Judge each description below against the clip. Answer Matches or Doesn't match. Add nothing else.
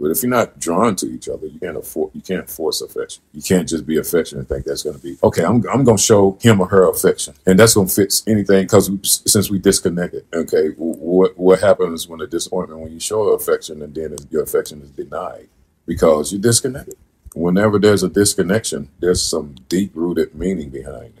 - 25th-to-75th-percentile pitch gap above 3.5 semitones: Matches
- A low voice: Matches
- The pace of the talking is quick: Matches